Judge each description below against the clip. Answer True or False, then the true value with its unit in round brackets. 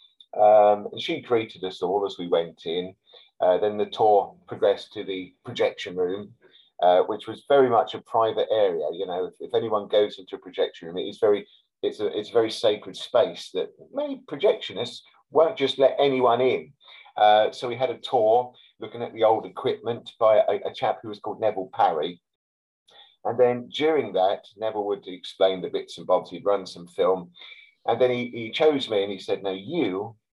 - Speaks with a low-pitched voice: True (125 Hz)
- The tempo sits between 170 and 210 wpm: True (200 wpm)